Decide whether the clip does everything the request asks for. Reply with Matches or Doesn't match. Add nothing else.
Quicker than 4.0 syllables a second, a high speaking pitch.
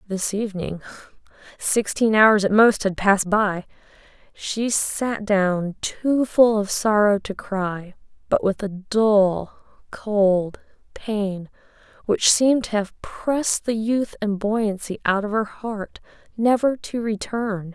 Doesn't match